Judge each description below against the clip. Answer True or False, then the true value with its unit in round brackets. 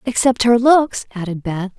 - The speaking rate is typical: True (170 wpm)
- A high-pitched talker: True (225 Hz)